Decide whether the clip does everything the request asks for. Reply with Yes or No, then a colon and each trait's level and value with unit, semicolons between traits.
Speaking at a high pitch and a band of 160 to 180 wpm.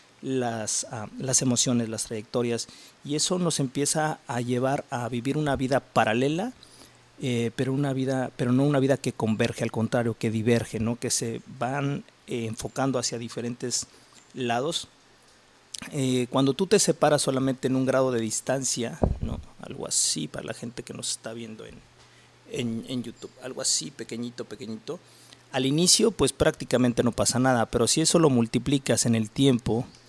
No: low, 125 Hz; average, 170 wpm